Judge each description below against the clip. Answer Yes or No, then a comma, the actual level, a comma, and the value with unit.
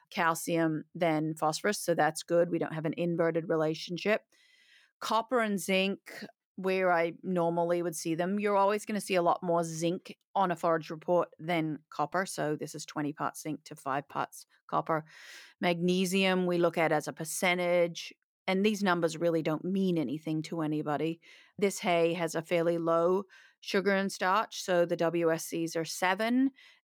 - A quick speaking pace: No, average, 170 wpm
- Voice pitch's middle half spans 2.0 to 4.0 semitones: Yes, narrow, 2.6 semitones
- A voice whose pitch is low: No, medium, 170 Hz